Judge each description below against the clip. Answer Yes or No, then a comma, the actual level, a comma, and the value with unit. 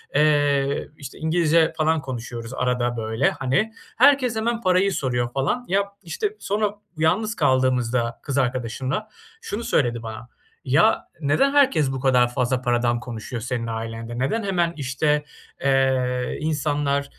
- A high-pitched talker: No, low, 135 Hz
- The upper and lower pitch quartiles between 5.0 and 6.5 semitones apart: Yes, wide, 5.6 semitones